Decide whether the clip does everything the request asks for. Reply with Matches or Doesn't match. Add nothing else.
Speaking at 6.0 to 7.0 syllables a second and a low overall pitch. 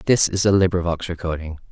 Matches